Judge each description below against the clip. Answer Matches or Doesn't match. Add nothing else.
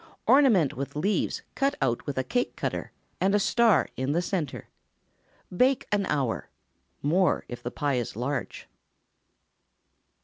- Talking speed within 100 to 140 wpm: Matches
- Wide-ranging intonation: Matches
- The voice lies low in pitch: Doesn't match